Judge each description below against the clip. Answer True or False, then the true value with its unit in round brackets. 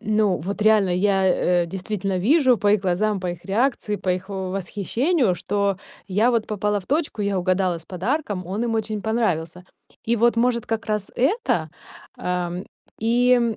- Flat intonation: False (3.6 semitones)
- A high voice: True (205 Hz)